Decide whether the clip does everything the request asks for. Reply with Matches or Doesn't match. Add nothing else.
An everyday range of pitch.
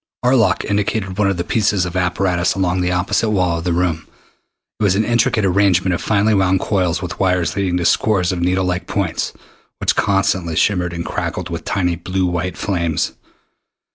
Doesn't match